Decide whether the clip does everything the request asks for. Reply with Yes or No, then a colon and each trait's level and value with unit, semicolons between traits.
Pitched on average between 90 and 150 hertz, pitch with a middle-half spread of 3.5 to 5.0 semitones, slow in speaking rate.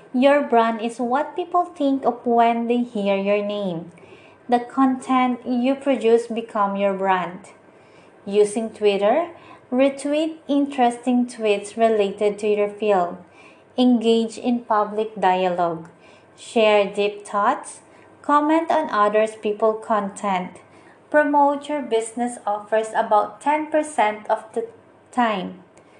No: high, 230 Hz; average, 4.0 semitones; slow, 115 wpm